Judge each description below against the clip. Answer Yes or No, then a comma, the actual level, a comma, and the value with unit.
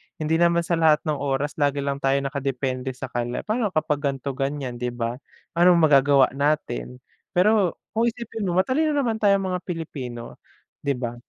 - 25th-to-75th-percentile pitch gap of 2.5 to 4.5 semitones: No, average, 4.9 semitones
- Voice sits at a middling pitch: Yes, medium, 145 Hz